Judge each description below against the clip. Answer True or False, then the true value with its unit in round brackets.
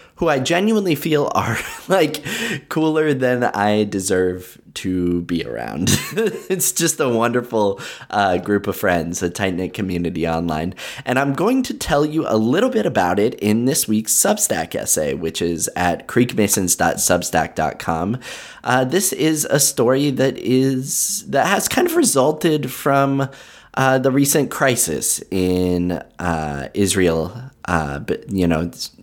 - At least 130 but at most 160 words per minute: True (145 wpm)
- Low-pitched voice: True (120 Hz)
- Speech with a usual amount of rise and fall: False (8.0 semitones)